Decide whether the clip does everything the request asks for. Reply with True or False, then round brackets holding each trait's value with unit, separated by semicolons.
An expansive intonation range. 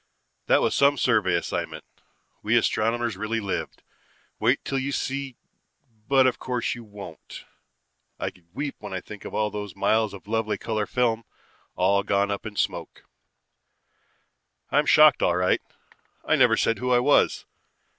False (4.0 semitones)